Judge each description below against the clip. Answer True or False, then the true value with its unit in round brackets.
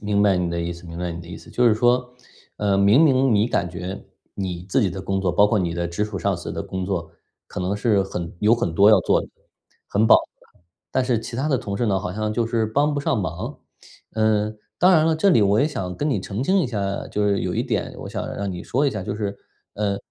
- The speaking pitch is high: False (105 Hz)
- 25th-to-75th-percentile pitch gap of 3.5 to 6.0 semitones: True (4.1 semitones)